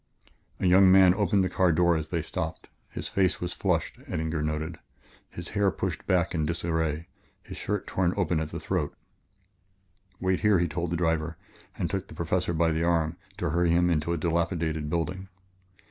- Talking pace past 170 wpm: Yes, average, 180 wpm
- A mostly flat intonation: Yes, narrow, 2.3 semitones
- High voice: No, very low, 85 Hz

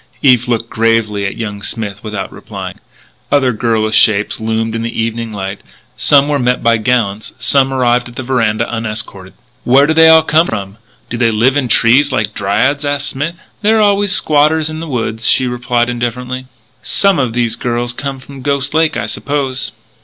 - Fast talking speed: No, average, 185 wpm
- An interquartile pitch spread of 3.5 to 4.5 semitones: Yes, average, 4.0 semitones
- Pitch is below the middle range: Yes, low, 120 Hz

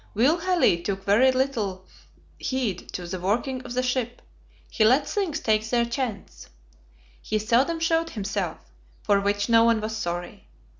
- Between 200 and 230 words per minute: No, average, 155 wpm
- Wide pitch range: No, average, 4.5 semitones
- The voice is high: Yes, high, 230 Hz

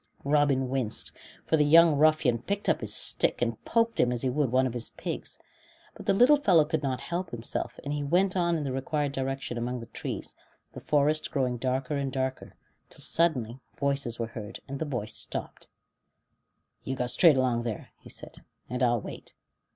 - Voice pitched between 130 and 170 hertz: Yes, low, 135 Hz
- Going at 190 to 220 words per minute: Yes, average, 195 wpm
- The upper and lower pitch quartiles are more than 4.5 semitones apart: No, average, 3.8 semitones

